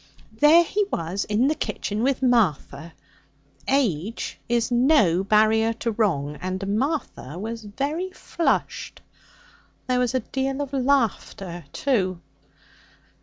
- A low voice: No, high, 230 Hz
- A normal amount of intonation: No, wide, 5.9 semitones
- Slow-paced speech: Yes, slow, 120 wpm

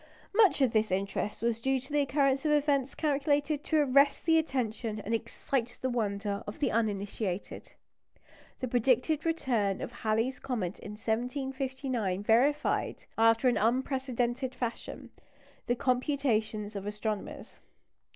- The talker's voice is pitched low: No, high, 245 Hz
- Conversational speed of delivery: No, slow, 130 wpm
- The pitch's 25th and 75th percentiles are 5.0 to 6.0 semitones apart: No, average, 4.0 semitones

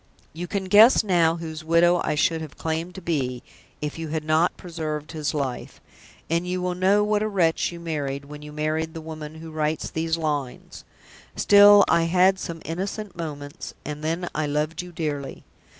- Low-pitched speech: No, medium, 160 Hz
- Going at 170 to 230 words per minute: Yes, average, 185 wpm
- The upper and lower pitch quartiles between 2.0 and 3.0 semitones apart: Yes, average, 2.7 semitones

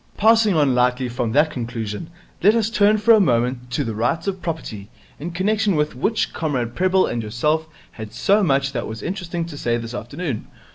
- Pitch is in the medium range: Yes, medium, 145 Hz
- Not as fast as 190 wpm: No, average, 195 wpm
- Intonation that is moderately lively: No, wide, 7.6 semitones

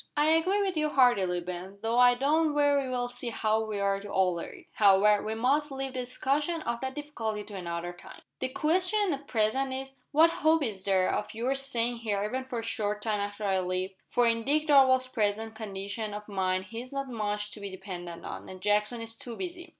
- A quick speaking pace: Yes, fast, 220 wpm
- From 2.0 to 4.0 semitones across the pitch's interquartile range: No, average, 5.0 semitones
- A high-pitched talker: Yes, high, 230 Hz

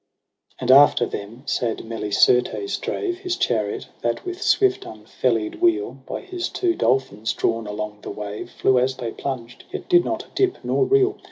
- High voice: No, low, 130 Hz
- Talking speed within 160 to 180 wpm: Yes, average, 165 wpm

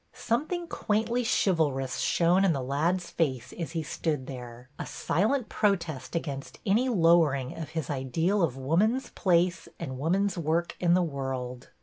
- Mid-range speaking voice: Yes, medium, 165 Hz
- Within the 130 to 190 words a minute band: Yes, average, 150 wpm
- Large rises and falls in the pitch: Yes, wide, 6.0 semitones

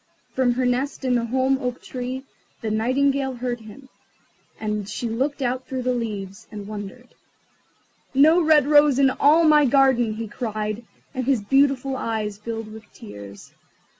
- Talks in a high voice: Yes, very high, 250 Hz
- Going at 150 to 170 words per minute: Yes, average, 160 wpm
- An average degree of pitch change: Yes, average, 3.7 semitones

